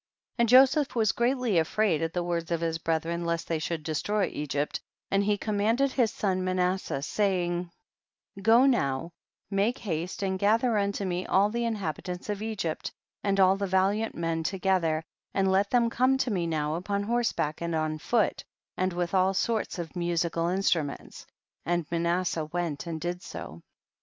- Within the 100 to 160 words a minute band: No, average, 175 wpm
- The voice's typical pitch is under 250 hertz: Yes, medium, 185 Hz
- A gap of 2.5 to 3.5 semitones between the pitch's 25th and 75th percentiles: No, average, 3.9 semitones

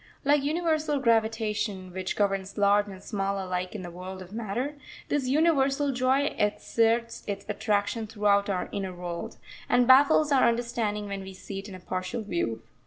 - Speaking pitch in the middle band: No, high, 210 Hz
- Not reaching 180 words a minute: Yes, average, 170 wpm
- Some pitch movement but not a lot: Yes, average, 4.7 semitones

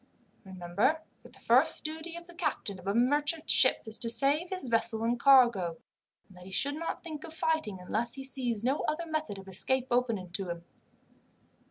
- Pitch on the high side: Yes, high, 245 Hz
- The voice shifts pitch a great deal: Yes, wide, 7.5 semitones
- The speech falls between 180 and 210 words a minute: Yes, average, 195 wpm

